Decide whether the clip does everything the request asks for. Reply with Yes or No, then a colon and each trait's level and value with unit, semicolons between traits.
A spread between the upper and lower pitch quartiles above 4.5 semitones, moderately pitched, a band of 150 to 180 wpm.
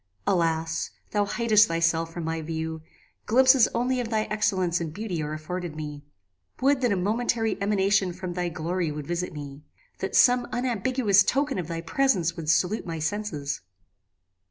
Yes: average, 5.2 semitones; medium, 180 Hz; average, 160 wpm